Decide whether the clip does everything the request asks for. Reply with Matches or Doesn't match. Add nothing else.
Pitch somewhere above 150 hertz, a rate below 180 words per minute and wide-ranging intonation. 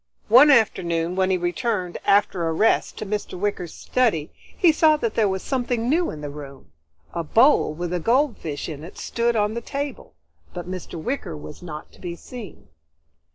Doesn't match